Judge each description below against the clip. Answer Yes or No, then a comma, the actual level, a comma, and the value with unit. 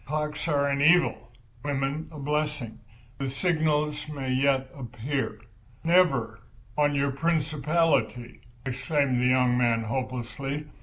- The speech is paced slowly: Yes, slow, 115 wpm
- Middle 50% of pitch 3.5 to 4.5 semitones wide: No, average, 2.9 semitones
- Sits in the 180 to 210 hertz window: No, medium, 140 Hz